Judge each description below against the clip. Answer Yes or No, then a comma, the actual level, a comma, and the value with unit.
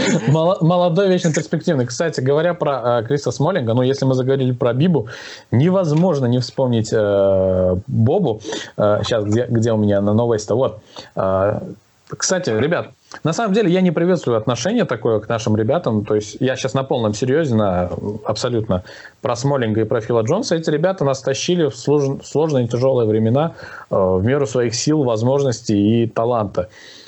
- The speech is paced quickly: Yes, fast, 170 wpm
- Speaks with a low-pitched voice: Yes, low, 125 Hz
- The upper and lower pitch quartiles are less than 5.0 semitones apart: No, average, 5.3 semitones